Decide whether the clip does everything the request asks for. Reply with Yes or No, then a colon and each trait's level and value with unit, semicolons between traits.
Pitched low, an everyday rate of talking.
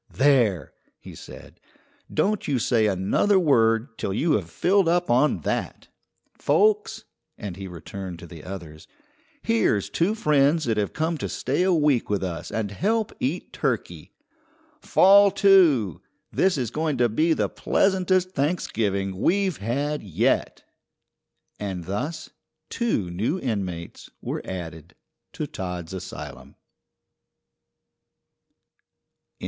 No: low, 125 Hz; slow, 125 wpm